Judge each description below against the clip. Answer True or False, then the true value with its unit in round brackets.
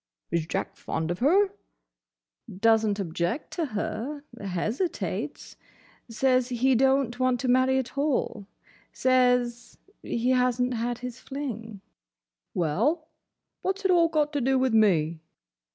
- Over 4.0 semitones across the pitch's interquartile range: False (3.7 semitones)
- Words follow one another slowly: True (130 wpm)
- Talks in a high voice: True (250 Hz)